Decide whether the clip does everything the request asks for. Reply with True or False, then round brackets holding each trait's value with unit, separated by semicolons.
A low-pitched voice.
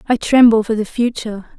False (225 Hz)